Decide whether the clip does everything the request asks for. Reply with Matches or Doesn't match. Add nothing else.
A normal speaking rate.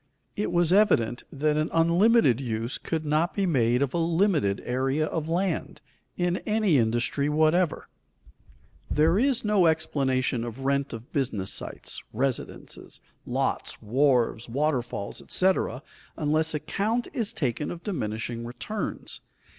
Doesn't match